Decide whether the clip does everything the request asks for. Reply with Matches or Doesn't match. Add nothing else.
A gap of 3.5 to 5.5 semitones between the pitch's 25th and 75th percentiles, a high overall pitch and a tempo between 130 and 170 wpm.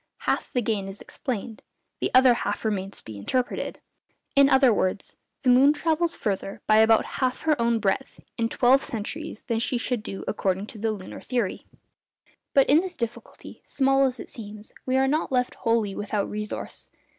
Doesn't match